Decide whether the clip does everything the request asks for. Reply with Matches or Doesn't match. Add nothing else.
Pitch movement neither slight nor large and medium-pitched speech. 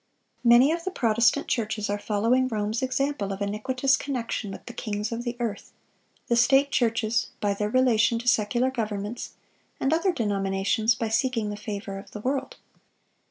Doesn't match